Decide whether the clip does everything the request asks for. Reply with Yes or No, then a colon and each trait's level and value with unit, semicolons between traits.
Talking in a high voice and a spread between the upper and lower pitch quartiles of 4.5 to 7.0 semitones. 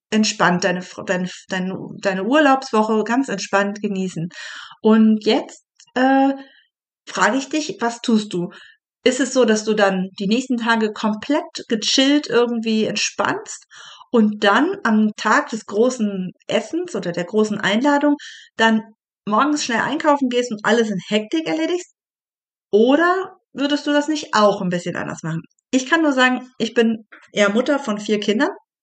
Yes: high, 225 Hz; average, 4.9 semitones